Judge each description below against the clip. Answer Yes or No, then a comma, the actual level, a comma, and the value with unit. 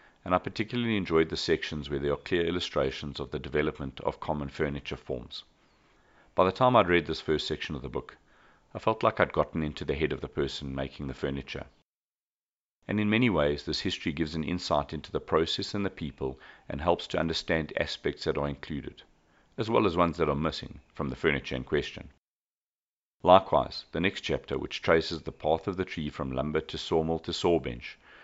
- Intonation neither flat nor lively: Yes, average, 3.7 semitones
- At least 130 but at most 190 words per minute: No, average, 200 wpm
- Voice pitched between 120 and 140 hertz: No, very low, 80 Hz